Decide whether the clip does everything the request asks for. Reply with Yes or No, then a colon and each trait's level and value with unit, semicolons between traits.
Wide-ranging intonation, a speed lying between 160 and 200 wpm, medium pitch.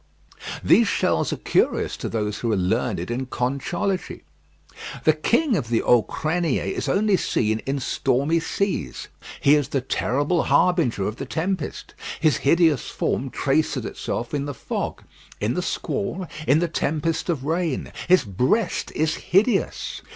No: wide, 5.8 semitones; average, 150 wpm; medium, 150 Hz